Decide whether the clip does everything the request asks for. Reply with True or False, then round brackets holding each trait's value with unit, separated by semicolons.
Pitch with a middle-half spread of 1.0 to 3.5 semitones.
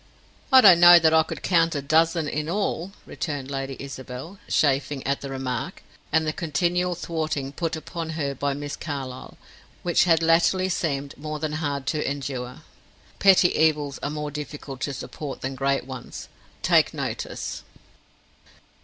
True (3.1 semitones)